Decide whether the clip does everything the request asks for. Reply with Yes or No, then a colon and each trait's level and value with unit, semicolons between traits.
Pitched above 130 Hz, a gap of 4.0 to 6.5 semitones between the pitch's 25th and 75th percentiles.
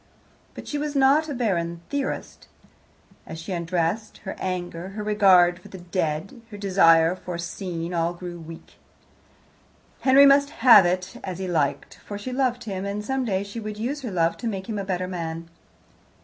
Yes: high, 190 Hz; average, 4.6 semitones